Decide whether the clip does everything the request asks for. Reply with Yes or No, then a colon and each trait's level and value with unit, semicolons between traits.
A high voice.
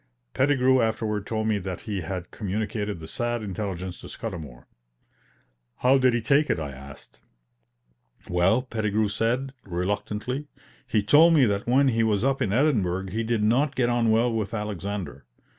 No: low, 110 Hz